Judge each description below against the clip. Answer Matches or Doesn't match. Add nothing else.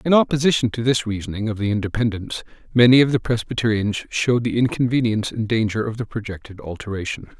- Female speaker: Doesn't match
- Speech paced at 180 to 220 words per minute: Doesn't match